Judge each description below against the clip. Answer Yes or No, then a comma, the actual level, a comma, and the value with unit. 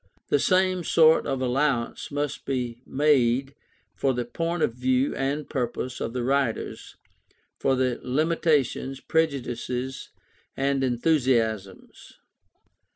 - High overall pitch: No, low, 135 Hz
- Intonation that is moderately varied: Yes, average, 3.0 semitones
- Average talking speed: No, slow, 110 wpm